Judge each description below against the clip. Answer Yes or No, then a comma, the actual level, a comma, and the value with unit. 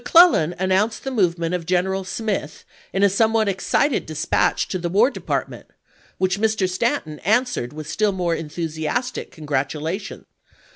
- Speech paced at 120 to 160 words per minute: Yes, average, 140 wpm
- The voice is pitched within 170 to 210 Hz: Yes, medium, 185 Hz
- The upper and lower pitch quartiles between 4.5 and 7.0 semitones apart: Yes, average, 5.0 semitones